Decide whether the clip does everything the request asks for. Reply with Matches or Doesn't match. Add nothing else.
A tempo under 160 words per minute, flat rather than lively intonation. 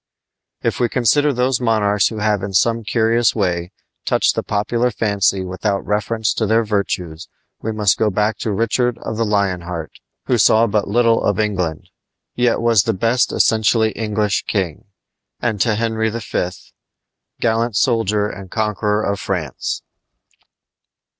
Matches